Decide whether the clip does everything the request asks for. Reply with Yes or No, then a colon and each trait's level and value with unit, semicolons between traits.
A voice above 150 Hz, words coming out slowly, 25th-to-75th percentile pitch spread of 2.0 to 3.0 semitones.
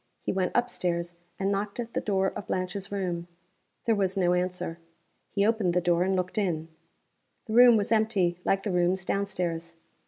No: high, 190 Hz; average, 190 wpm; narrow, 2.4 semitones